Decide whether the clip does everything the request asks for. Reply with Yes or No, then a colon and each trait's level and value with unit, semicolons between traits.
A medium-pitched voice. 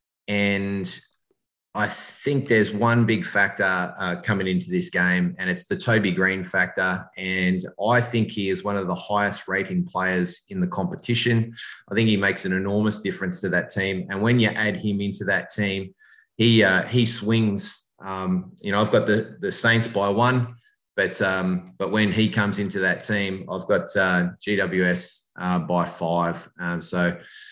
No: low, 100 Hz